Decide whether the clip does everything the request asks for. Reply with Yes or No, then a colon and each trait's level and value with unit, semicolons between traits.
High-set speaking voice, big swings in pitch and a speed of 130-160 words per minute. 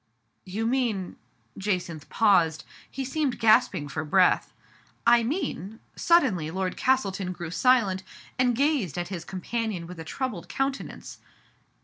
Yes: high, 195 Hz; wide, 6.4 semitones; average, 145 wpm